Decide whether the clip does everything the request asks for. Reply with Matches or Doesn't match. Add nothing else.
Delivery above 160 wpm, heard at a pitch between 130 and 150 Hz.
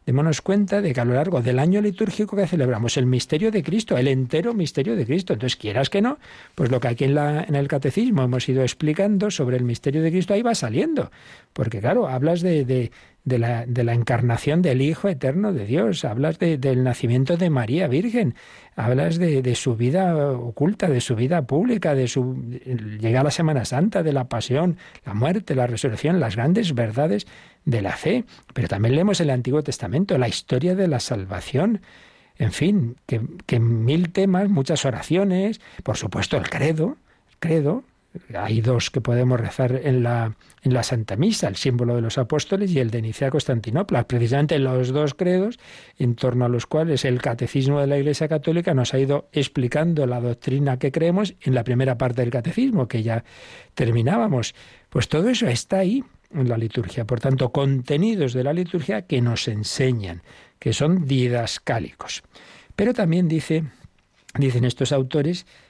Matches